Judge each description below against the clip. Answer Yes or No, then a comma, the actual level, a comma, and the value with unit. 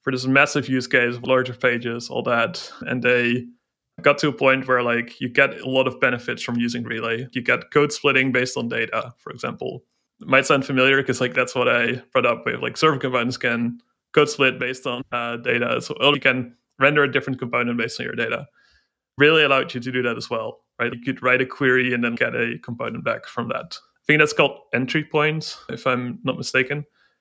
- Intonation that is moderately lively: No, narrow, 2.2 semitones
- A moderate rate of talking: No, fast, 225 wpm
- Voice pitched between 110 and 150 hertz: Yes, low, 130 Hz